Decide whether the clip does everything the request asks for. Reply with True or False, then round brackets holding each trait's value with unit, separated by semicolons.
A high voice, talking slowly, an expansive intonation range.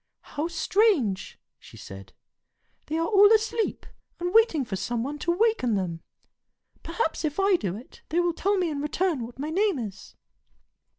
False (320 Hz; 170 wpm; 8.2 semitones)